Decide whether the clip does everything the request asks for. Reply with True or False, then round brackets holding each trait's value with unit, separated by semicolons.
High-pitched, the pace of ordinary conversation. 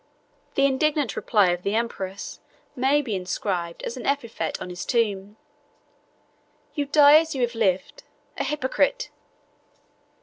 False (235 Hz; 130 wpm)